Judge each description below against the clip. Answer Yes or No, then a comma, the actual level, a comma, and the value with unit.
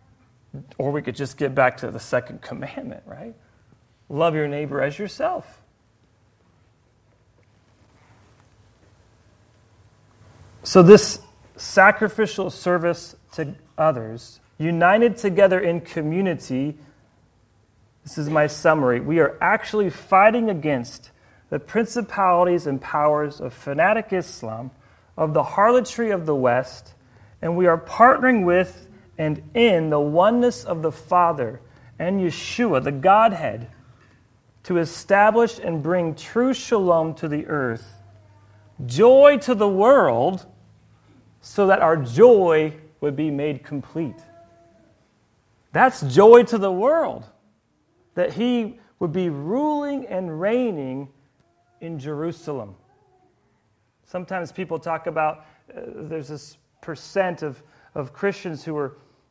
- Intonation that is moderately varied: No, wide, 7.4 semitones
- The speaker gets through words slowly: Yes, slow, 115 wpm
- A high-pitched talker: No, medium, 150 Hz